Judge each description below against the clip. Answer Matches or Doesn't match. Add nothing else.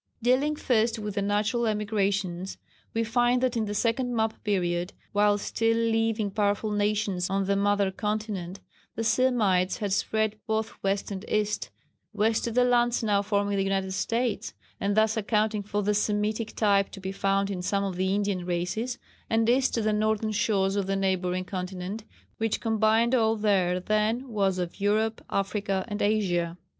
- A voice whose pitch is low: Doesn't match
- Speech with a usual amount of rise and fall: Doesn't match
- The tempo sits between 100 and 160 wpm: Doesn't match